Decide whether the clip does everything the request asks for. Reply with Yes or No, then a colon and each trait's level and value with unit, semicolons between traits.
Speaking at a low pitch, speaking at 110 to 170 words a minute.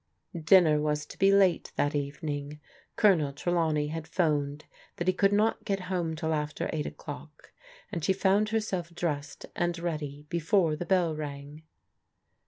No: medium, 160 Hz; average, 160 wpm